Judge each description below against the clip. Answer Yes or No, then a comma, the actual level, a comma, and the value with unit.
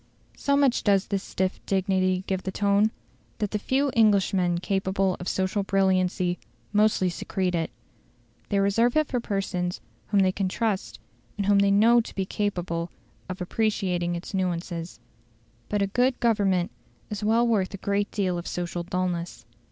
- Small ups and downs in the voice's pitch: Yes, narrow, 2.3 semitones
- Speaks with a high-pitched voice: Yes, high, 195 Hz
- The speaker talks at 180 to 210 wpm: No, average, 160 wpm